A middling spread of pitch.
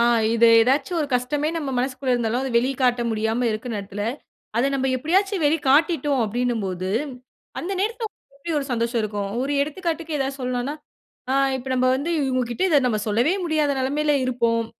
Yes: average, 4.0 semitones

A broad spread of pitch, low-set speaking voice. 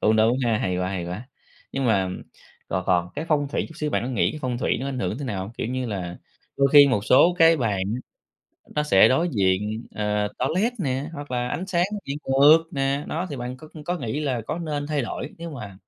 Yes: wide, 6.0 semitones; low, 130 Hz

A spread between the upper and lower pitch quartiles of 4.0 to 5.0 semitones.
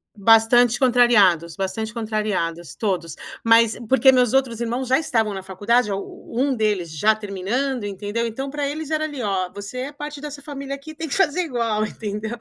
Yes: average, 4.7 semitones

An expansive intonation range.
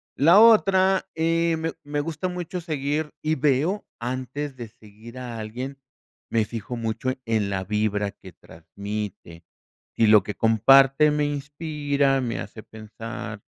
Yes: wide, 5.7 semitones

